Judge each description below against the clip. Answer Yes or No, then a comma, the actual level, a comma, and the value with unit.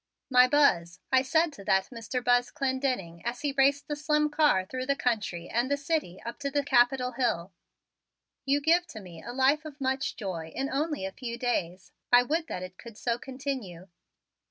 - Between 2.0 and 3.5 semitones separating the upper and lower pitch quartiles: No, wide, 5.4 semitones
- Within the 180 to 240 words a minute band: Yes, average, 195 wpm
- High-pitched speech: Yes, very high, 255 Hz